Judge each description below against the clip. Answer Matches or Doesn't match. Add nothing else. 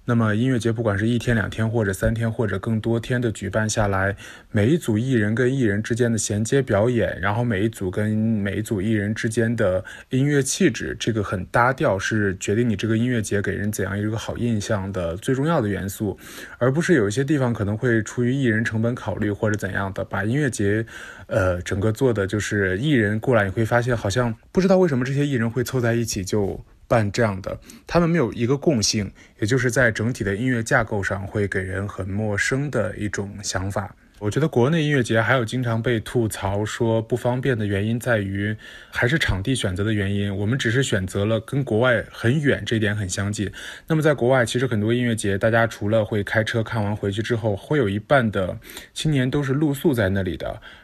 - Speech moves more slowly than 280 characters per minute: Doesn't match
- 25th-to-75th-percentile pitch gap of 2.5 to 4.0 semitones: Matches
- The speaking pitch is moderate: Doesn't match